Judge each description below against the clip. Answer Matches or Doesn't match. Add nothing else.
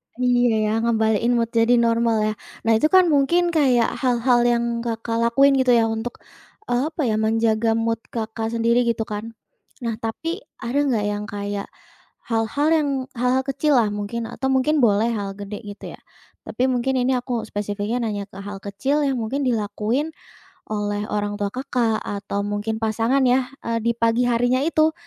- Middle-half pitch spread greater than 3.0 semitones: Doesn't match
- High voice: Matches